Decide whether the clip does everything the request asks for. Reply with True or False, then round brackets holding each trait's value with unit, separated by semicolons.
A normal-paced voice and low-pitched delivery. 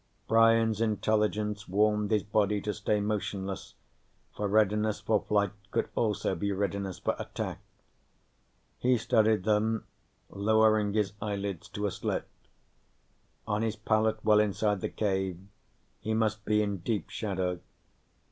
False (130 wpm; 105 Hz)